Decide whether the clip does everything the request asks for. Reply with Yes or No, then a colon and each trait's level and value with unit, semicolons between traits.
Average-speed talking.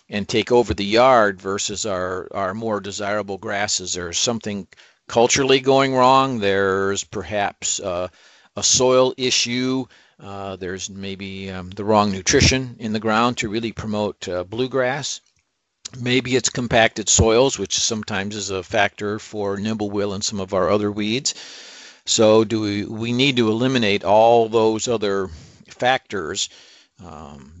Yes: average, 145 wpm